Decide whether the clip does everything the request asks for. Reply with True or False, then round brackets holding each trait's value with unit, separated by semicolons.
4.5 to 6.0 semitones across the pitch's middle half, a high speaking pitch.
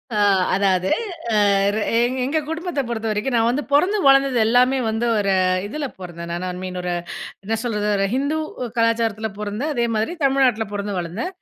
True (5.0 semitones; 225 Hz)